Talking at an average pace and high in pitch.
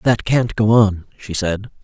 No: average, 195 wpm; low, 105 Hz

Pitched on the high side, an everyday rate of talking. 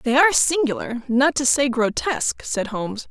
Yes: very high, 265 Hz; average, 175 wpm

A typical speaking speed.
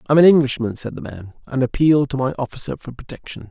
No: fast, 240 wpm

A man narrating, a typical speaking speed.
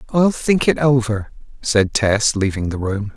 Yes: male; average, 170 wpm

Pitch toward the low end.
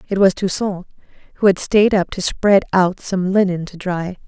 No: high, 190 Hz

